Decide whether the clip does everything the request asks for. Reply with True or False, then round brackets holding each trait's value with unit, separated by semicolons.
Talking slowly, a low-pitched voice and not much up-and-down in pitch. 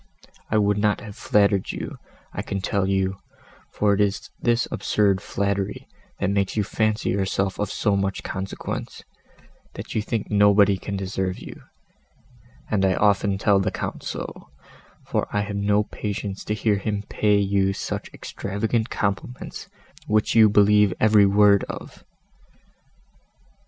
False (145 wpm; 100 Hz; 1.2 semitones)